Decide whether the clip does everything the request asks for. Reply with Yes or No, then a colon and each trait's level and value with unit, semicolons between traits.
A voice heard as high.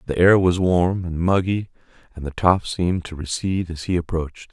No: very low, 85 Hz